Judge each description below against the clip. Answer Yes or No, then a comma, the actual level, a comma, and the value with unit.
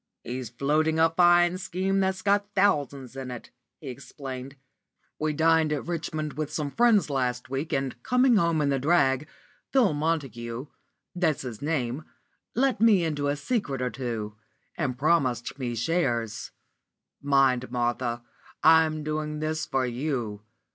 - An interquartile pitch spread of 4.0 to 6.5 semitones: Yes, average, 4.3 semitones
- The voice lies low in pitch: No, medium, 145 Hz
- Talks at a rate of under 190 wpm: Yes, average, 145 wpm